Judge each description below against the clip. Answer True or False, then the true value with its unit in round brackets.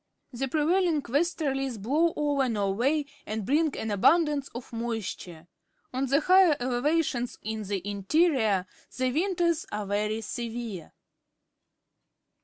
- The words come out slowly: True (115 wpm)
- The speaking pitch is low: False (255 Hz)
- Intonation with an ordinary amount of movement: False (6.0 semitones)